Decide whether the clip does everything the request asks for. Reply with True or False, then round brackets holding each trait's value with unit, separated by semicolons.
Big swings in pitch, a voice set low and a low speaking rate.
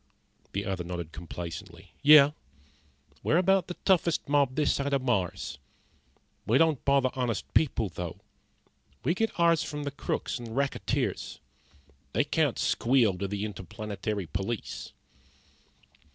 True (6.9 semitones; 125 Hz; 130 wpm)